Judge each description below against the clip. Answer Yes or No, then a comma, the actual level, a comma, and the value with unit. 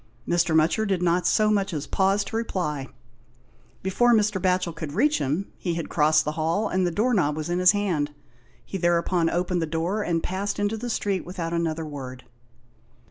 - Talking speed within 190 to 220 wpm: Yes, fast, 205 wpm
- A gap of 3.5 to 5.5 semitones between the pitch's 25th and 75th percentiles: Yes, average, 3.9 semitones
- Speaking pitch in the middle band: Yes, medium, 175 Hz